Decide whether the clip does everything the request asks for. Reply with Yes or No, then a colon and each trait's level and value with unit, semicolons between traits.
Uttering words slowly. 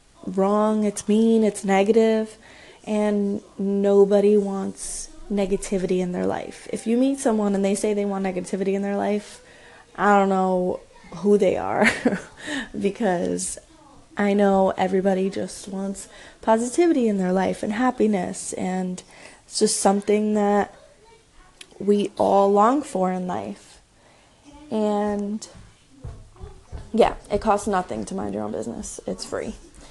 Yes: slow, 130 wpm